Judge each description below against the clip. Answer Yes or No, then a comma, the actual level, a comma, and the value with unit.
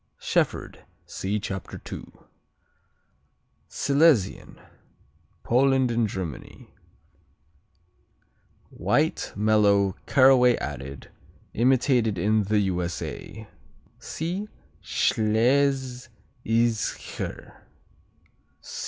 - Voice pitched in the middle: No, low, 115 Hz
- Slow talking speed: Yes, slow, 55 wpm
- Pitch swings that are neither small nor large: Yes, average, 4.5 semitones